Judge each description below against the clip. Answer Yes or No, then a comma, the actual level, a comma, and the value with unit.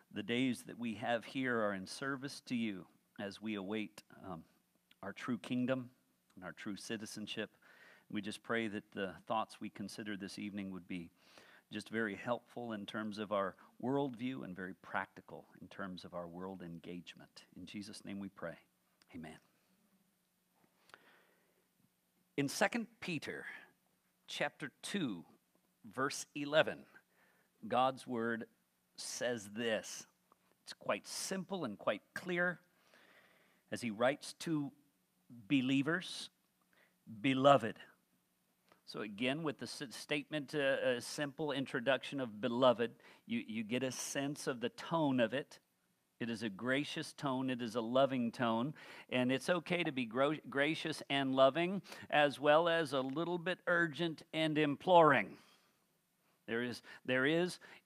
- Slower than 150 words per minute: Yes, average, 140 wpm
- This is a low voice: Yes, low, 130 Hz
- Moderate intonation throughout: No, wide, 5.8 semitones